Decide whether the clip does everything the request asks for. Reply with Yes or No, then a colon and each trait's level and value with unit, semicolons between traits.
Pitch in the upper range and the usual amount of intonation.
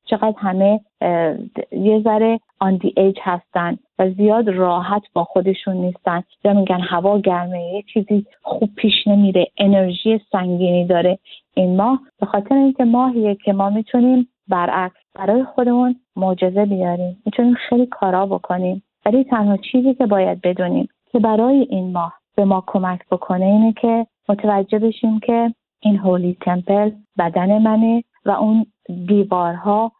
Yes: high, 205 Hz; average, 3.3 semitones